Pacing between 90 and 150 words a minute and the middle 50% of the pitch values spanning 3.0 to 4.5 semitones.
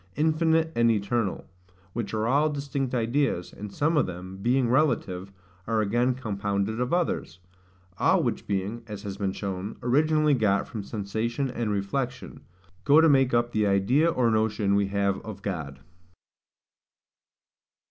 No: average, 145 wpm; average, 5.0 semitones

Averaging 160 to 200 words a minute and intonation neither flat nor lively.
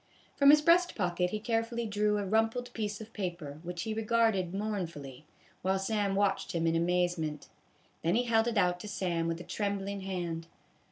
Yes: average, 180 wpm; average, 4.1 semitones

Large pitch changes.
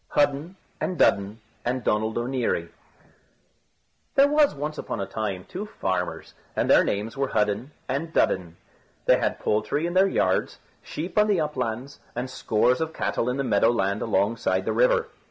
Yes: wide, 7.2 semitones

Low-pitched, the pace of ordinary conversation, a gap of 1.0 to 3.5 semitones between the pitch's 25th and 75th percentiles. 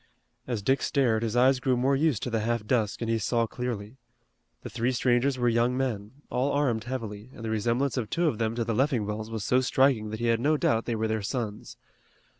No: low, 120 Hz; fast, 230 wpm; average, 2.7 semitones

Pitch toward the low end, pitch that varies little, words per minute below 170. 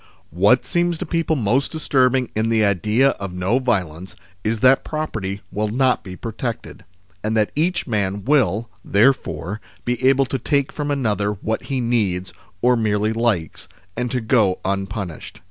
No: low, 115 Hz; average, 4.6 semitones; average, 160 wpm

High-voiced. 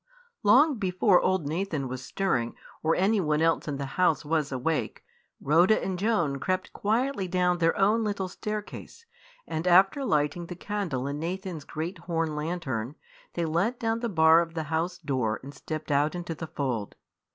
No: medium, 170 Hz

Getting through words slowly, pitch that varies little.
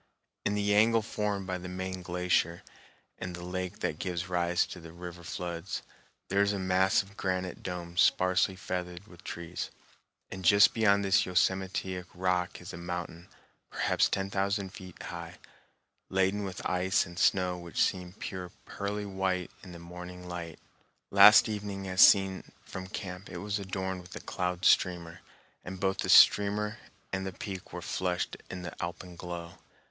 No: average, 165 wpm; narrow, 1.7 semitones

